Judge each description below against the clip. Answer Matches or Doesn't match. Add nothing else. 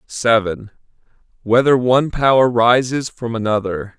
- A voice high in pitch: Doesn't match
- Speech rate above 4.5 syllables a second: Matches